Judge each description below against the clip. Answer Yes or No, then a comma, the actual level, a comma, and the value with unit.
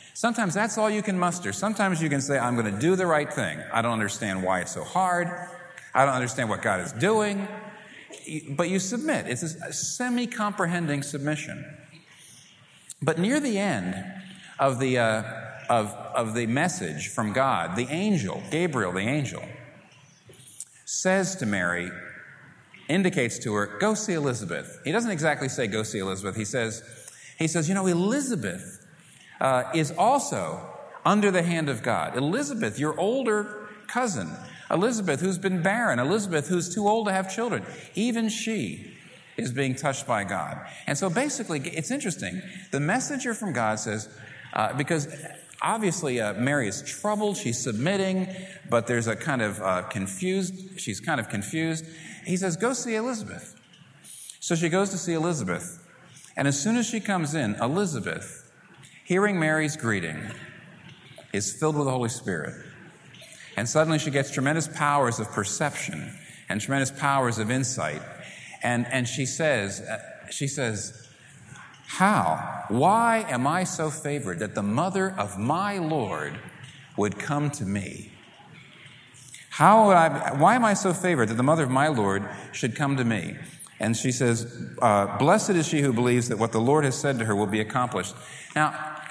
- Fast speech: No, average, 165 wpm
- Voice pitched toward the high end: No, medium, 150 Hz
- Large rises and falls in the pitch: Yes, wide, 7.6 semitones